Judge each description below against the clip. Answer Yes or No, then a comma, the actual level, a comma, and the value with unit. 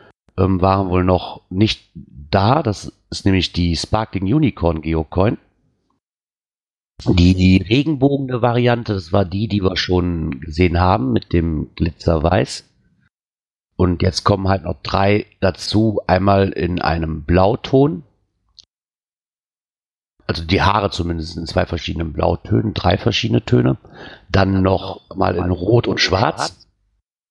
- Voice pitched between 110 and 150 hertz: No, very low, 95 Hz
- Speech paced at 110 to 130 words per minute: Yes, slow, 125 wpm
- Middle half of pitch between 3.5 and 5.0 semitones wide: No, average, 3.1 semitones